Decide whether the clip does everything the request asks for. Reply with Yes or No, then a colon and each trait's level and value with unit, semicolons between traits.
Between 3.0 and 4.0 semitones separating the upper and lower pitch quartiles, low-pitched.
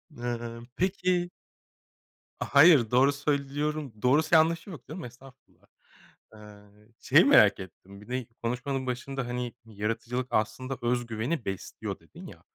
Yes: average, 3.7 semitones; low, 125 Hz